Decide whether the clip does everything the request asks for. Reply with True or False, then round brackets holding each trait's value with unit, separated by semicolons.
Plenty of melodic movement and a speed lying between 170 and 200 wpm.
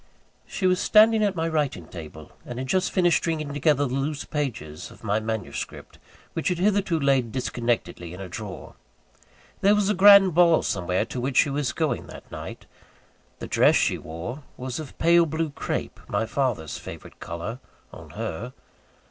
True (7.4 semitones; 175 wpm)